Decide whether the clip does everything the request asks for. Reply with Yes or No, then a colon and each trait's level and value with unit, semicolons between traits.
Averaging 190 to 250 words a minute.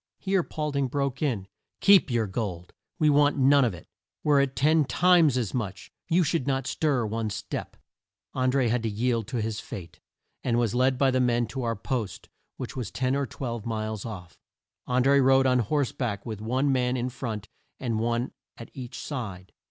Yes: average, 200 wpm